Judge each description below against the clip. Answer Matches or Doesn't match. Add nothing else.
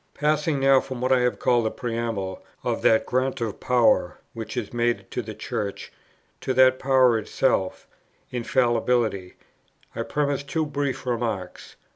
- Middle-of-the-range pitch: Doesn't match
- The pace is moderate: Matches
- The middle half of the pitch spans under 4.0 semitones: Matches